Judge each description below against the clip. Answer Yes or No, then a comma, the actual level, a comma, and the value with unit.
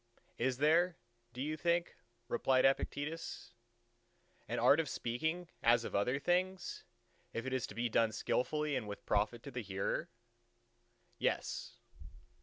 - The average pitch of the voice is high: No, low, 130 Hz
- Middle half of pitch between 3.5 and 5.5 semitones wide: Yes, average, 5.2 semitones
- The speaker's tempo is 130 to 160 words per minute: Yes, average, 140 wpm